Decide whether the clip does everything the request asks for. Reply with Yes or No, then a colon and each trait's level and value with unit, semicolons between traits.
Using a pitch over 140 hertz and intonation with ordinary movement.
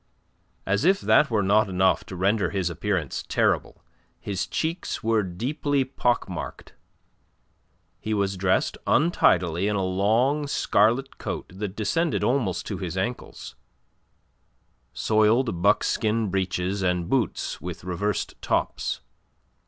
No: low, 100 Hz; average, 4.4 semitones